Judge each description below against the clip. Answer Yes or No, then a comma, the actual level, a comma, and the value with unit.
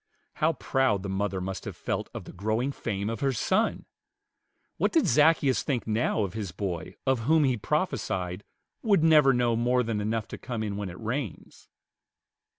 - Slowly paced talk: No, average, 180 wpm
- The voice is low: Yes, low, 115 Hz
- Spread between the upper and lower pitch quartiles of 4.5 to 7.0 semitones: Yes, average, 5.0 semitones